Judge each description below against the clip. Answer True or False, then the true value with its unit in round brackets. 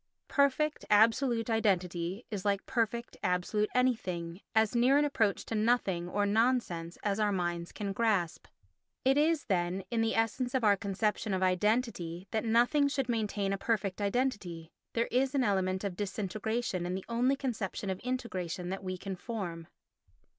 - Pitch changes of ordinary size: True (4.2 semitones)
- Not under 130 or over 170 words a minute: True (160 wpm)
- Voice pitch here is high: True (210 Hz)